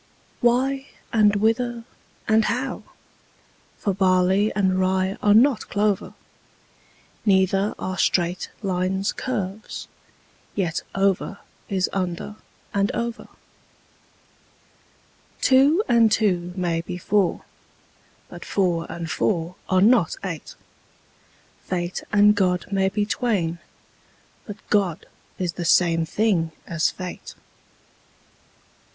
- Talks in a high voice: Yes, high, 195 Hz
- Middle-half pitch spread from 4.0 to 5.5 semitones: No, average, 3.1 semitones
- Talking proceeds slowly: Yes, slow, 105 wpm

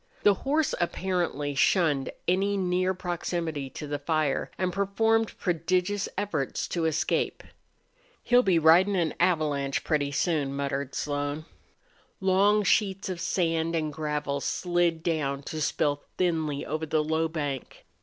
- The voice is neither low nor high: Yes, medium, 165 Hz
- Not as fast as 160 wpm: Yes, slow, 135 wpm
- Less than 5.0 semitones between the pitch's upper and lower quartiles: Yes, average, 4.0 semitones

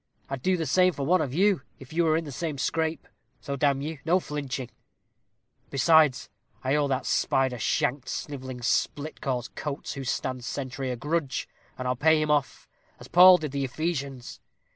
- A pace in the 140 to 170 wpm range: No, average, 185 wpm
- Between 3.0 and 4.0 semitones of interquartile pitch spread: Yes, average, 3.3 semitones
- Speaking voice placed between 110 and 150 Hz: Yes, medium, 140 Hz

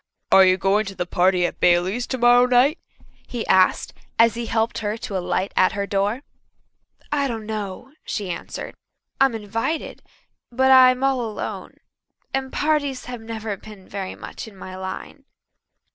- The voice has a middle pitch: No, high, 220 Hz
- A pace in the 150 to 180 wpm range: Yes, average, 160 wpm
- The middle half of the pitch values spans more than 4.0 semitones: Yes, average, 4.7 semitones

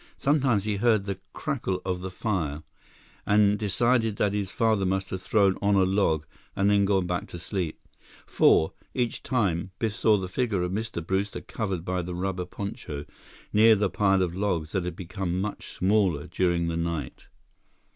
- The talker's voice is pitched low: Yes, very low, 95 Hz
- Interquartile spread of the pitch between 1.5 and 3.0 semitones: Yes, average, 2.7 semitones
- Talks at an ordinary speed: Yes, average, 175 wpm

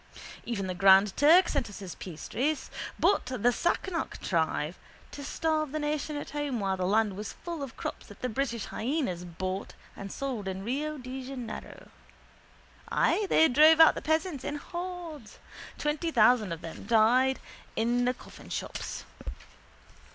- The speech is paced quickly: No, average, 155 wpm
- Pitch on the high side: Yes, very high, 250 Hz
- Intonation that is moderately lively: No, wide, 6.8 semitones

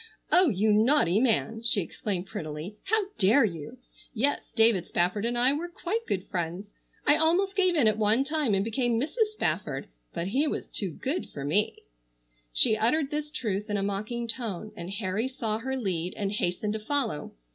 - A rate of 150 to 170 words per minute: No, average, 185 wpm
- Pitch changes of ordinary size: No, wide, 5.7 semitones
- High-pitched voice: Yes, high, 220 Hz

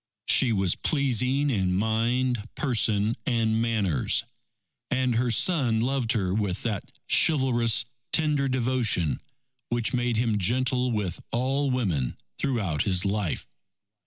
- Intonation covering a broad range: No, average, 3.8 semitones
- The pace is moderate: No, slow, 120 wpm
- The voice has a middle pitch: No, low, 115 Hz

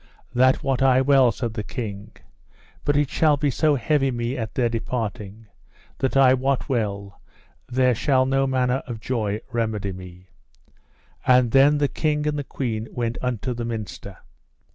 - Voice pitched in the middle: No, low, 125 Hz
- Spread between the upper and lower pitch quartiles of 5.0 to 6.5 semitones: No, average, 3.4 semitones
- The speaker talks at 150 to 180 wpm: Yes, average, 160 wpm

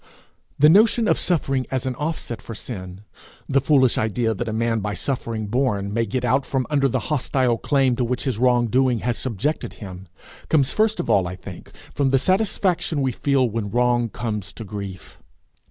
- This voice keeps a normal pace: Yes, average, 190 wpm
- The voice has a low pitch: Yes, low, 125 Hz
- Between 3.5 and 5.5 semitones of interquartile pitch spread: Yes, average, 3.9 semitones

